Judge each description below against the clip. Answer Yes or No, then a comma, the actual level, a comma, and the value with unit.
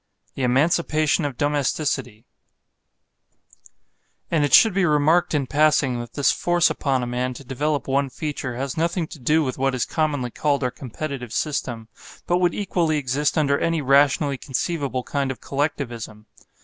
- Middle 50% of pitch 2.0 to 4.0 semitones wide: Yes, average, 3.2 semitones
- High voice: No, medium, 140 Hz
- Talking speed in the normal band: Yes, average, 160 wpm